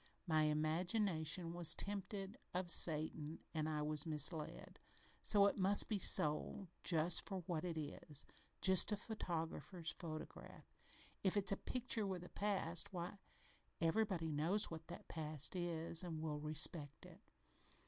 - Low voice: No, medium, 170 Hz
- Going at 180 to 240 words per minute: No, average, 140 wpm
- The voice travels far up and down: No, average, 3.6 semitones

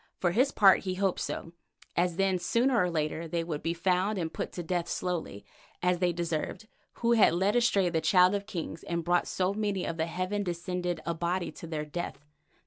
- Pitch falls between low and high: Yes, medium, 180 Hz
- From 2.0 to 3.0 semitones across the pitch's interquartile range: Yes, narrow, 2.5 semitones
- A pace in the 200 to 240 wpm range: Yes, fast, 205 wpm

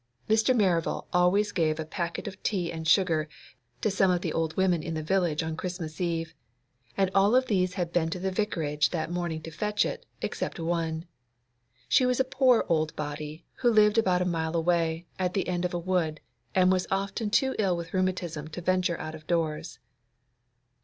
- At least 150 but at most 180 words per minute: No, average, 195 wpm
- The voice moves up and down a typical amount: Yes, average, 3.0 semitones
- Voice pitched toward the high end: No, medium, 175 Hz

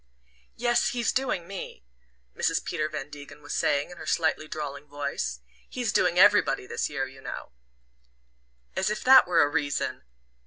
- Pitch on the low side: No, medium, 150 Hz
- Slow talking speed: No, average, 165 wpm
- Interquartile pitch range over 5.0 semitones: No, average, 4.2 semitones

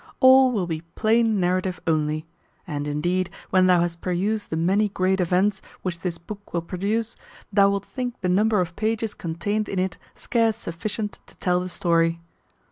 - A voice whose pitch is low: No, medium, 185 Hz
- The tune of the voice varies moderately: Yes, average, 3.8 semitones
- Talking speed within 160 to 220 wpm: Yes, average, 175 wpm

